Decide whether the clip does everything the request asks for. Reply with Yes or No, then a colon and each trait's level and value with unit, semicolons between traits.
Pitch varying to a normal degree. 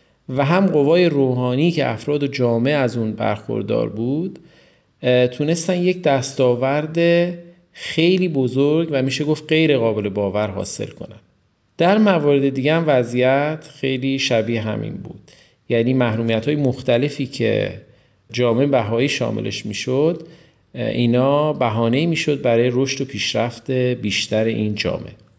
Yes: average, 4.3 semitones